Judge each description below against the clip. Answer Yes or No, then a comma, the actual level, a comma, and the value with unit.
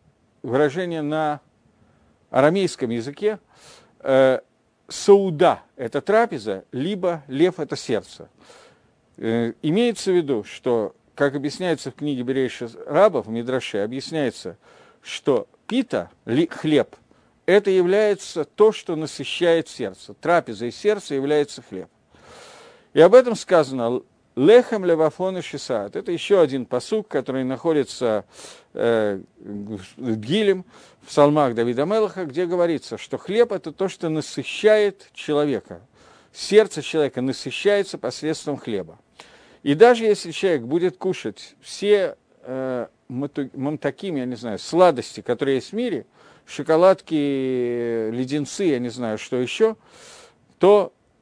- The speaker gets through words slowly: No, average, 120 wpm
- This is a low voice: No, medium, 150 Hz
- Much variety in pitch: Yes, wide, 7.0 semitones